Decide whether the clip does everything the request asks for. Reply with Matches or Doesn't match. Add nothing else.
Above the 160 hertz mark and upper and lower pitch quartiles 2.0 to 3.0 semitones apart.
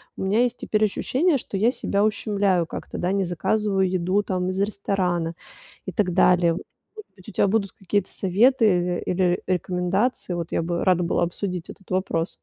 Matches